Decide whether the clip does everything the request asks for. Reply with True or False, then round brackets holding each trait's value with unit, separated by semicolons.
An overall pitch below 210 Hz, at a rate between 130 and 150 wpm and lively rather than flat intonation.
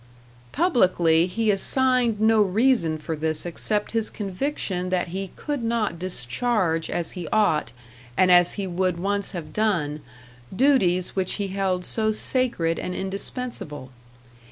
False (190 Hz; 135 wpm; 4.3 semitones)